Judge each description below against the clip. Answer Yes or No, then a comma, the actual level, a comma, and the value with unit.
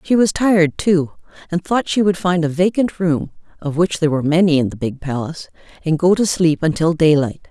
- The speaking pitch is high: No, medium, 165 Hz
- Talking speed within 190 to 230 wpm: Yes, average, 200 wpm